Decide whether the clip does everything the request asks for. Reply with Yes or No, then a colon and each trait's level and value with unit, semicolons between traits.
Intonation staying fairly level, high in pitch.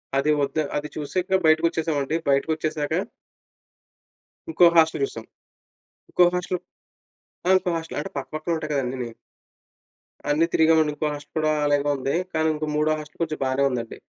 No: narrow, 2.1 semitones; medium, 155 Hz